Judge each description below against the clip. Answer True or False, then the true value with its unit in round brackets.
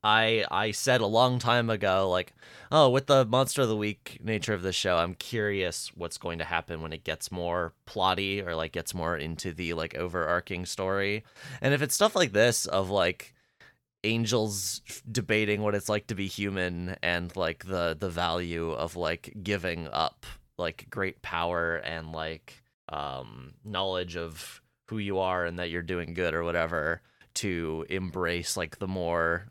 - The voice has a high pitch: False (95 Hz)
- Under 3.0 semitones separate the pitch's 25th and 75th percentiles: False (4.0 semitones)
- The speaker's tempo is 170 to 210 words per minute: True (180 wpm)